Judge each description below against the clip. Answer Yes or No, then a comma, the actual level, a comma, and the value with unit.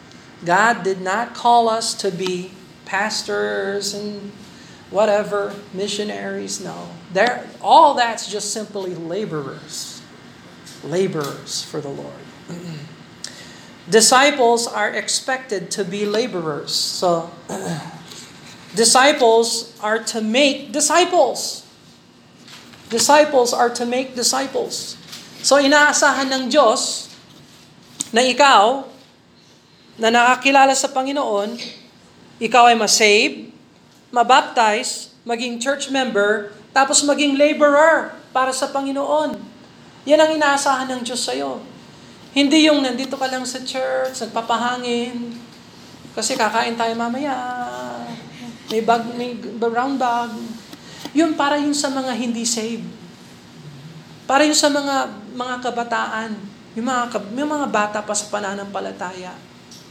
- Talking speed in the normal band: No, slow, 105 wpm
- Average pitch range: Yes, average, 4.4 semitones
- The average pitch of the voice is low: No, high, 235 Hz